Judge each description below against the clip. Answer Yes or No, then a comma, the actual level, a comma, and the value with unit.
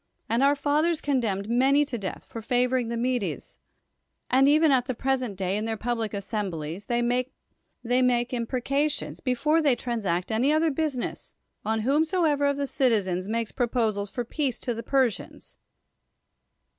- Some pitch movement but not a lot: Yes, average, 3.8 semitones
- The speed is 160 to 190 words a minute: No, average, 150 wpm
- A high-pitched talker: Yes, high, 245 Hz